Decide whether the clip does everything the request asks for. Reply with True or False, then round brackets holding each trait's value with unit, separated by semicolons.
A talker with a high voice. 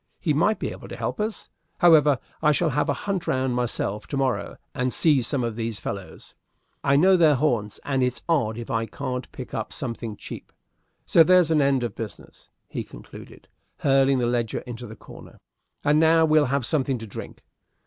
False (135 Hz)